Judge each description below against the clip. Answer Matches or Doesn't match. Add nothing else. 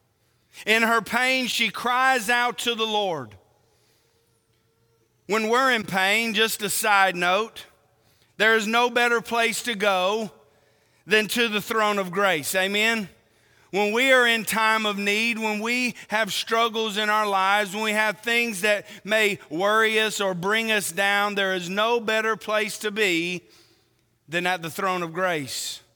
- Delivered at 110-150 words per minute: Doesn't match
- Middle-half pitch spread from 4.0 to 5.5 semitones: Matches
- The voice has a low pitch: Doesn't match